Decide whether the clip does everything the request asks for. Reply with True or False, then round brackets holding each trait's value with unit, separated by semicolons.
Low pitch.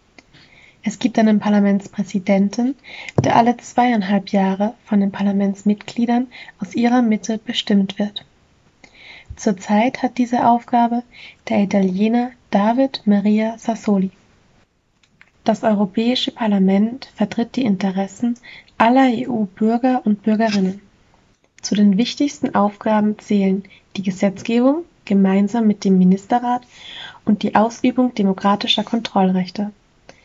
False (215 Hz)